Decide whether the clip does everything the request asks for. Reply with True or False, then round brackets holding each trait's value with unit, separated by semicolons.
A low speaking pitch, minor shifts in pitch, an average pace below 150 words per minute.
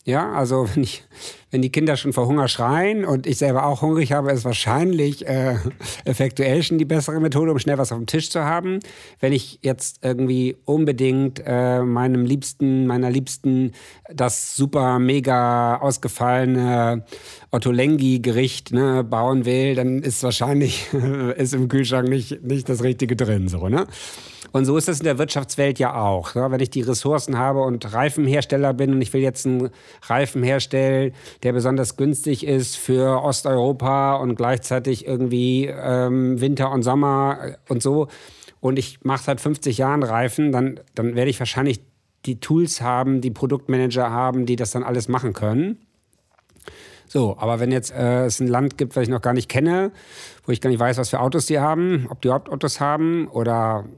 False (130 Hz; 2.0 semitones; 175 wpm)